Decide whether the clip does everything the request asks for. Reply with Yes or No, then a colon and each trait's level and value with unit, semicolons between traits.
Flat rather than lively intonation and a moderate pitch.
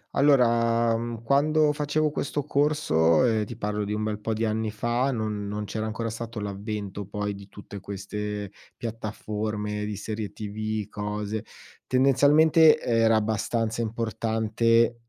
No: narrow, 2.1 semitones; low, 110 Hz